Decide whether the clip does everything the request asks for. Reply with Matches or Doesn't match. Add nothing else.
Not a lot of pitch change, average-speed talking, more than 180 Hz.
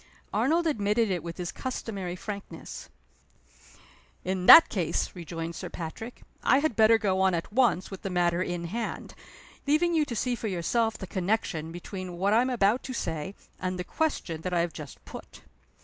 Doesn't match